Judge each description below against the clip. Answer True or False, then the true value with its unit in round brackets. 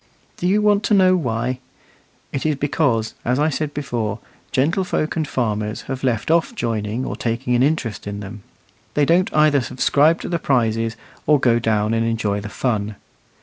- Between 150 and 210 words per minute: True (180 wpm)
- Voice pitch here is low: True (125 Hz)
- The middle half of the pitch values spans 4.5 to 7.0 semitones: True (5.3 semitones)